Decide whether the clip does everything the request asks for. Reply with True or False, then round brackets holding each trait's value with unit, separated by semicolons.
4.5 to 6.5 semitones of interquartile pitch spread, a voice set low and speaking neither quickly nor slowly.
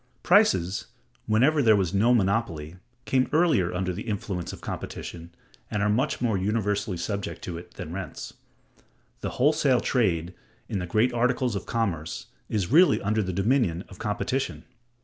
True (5.0 semitones; 105 Hz; 155 wpm)